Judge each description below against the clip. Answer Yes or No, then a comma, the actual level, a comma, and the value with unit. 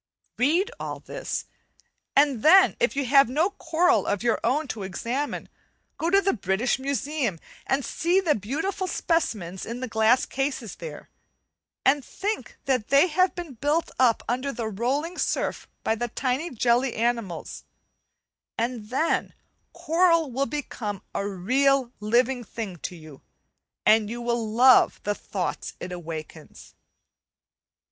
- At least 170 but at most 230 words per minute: No, average, 140 wpm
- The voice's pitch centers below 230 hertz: No, very high, 255 Hz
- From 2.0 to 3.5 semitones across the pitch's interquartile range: No, wide, 5.5 semitones